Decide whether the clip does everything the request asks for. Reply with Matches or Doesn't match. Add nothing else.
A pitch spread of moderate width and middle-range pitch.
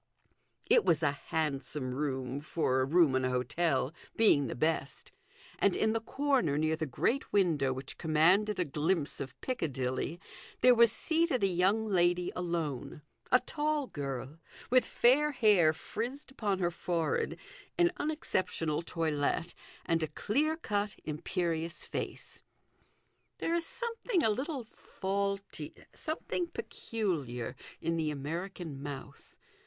Doesn't match